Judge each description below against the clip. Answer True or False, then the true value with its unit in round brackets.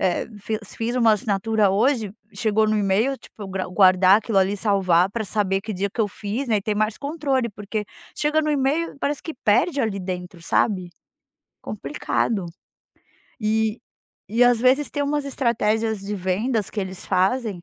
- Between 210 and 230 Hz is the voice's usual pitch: True (215 Hz)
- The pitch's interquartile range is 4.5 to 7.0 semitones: False (3.9 semitones)